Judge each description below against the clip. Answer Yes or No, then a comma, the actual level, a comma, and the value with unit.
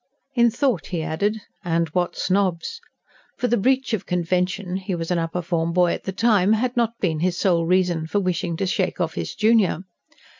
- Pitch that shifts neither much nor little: Yes, average, 3.8 semitones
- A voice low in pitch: No, medium, 185 Hz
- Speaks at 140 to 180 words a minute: No, average, 195 wpm